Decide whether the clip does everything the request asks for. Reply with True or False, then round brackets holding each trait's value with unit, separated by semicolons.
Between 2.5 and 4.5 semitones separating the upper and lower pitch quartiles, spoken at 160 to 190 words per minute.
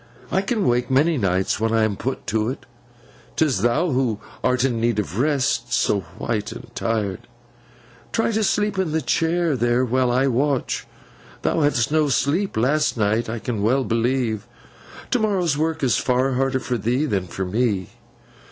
False (4.9 semitones; 170 wpm)